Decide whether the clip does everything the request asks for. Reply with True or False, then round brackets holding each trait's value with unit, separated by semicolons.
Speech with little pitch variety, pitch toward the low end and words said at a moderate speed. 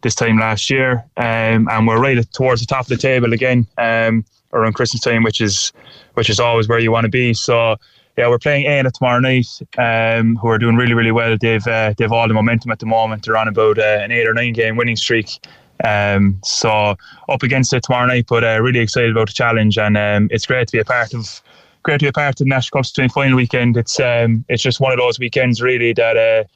False (1.9 semitones; 115 Hz; 245 wpm)